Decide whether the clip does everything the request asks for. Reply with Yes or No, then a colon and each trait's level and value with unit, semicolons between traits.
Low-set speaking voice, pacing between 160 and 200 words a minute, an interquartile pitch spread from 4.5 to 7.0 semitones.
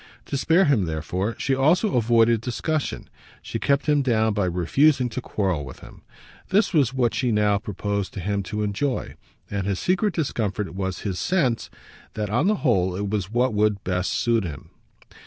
Yes: low, 110 Hz; average, 180 wpm; average, 5.3 semitones